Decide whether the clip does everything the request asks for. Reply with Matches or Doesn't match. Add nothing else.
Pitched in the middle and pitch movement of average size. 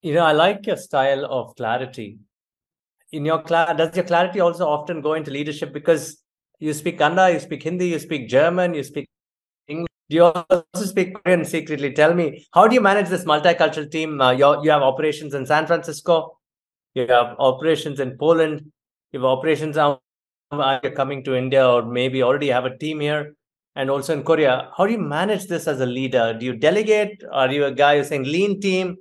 Matches